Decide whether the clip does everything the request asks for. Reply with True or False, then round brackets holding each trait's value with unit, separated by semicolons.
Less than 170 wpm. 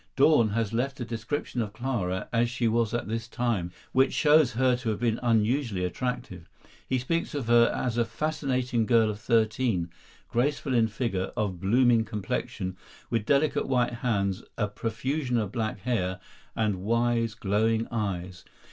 True (160 wpm)